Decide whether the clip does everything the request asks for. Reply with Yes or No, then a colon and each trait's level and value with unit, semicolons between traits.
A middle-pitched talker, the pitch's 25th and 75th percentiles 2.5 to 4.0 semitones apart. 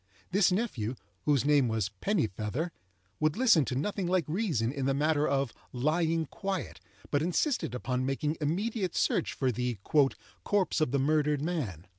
No: medium, 150 Hz; average, 5.3 semitones